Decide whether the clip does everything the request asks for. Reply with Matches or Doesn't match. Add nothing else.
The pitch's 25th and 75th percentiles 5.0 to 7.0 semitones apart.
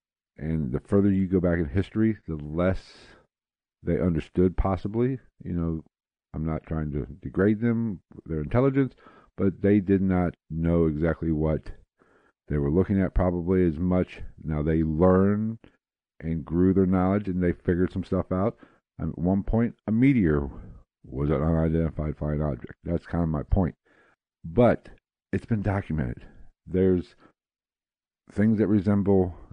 Doesn't match